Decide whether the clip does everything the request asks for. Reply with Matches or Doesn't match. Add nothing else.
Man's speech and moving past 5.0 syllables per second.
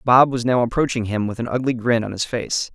Matches